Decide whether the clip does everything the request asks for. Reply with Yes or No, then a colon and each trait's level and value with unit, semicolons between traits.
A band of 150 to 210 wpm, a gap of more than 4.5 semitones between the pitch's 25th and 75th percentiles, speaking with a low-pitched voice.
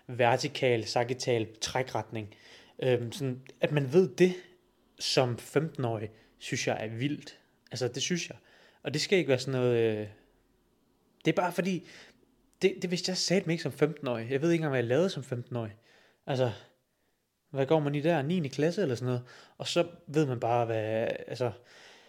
Yes: average, 180 wpm; average, 5.1 semitones; low, 130 Hz